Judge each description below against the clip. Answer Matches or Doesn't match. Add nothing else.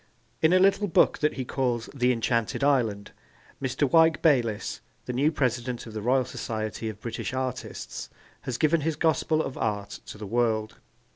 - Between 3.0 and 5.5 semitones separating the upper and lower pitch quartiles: Matches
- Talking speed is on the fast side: Doesn't match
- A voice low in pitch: Matches